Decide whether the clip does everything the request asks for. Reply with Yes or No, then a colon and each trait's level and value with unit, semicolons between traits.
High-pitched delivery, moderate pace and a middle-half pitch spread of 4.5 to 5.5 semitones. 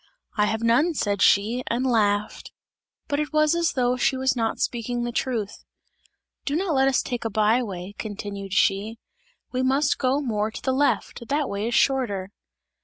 No: high, 240 Hz; average, 180 wpm; average, 4.1 semitones